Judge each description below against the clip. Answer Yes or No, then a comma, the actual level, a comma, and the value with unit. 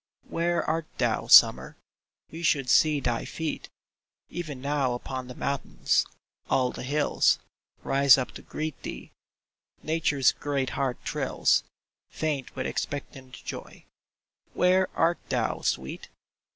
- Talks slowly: Yes, slow, 125 wpm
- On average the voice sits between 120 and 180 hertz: Yes, medium, 140 Hz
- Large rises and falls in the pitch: No, average, 3.3 semitones